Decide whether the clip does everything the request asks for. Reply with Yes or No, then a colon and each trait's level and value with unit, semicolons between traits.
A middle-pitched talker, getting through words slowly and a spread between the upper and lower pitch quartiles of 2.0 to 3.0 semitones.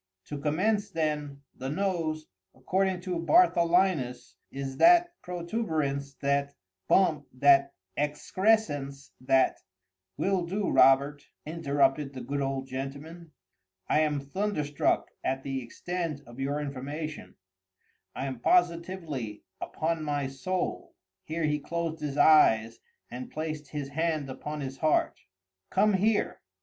No: medium, 150 Hz; slow, 105 wpm; average, 3.7 semitones